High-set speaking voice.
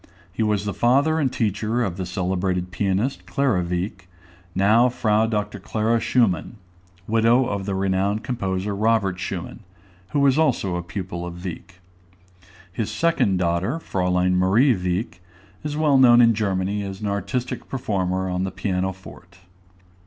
No: low, 100 Hz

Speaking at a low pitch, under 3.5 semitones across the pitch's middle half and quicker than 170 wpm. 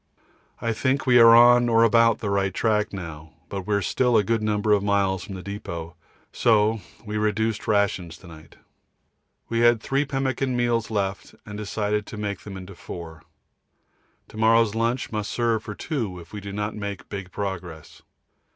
Yes: low, 105 Hz; average, 2.9 semitones; average, 180 wpm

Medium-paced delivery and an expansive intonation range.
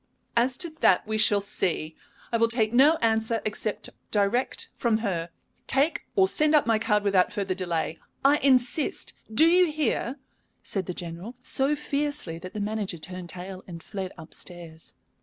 Yes: average, 170 wpm; wide, 6.3 semitones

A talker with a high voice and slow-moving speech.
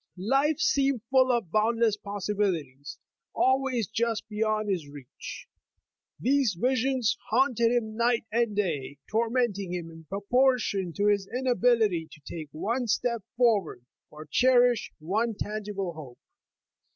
Yes: high, 215 Hz; slow, 125 wpm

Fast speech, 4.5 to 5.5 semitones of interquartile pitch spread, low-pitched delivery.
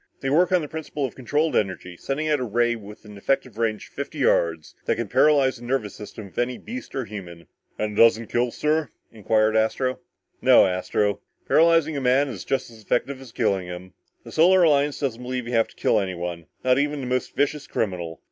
Yes: fast, 220 wpm; average, 5.1 semitones; low, 120 Hz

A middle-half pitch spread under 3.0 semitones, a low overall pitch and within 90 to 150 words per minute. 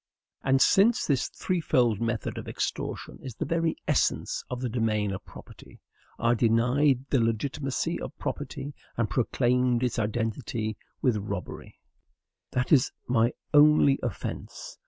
No: average, 3.4 semitones; low, 125 Hz; slow, 135 wpm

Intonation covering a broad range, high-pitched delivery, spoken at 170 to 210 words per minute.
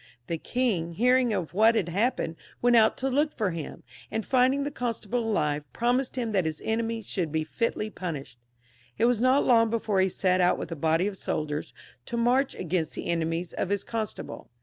Yes: wide, 6.1 semitones; high, 215 Hz; average, 195 wpm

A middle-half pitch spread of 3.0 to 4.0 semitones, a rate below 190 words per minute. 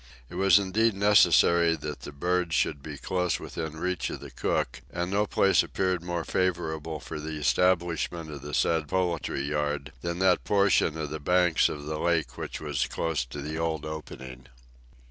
Yes: average, 3.3 semitones; average, 180 wpm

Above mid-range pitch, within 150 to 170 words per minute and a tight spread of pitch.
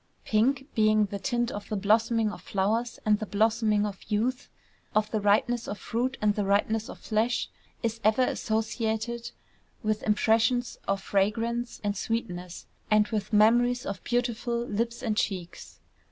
Yes: high, 220 Hz; average, 155 wpm; narrow, 2.2 semitones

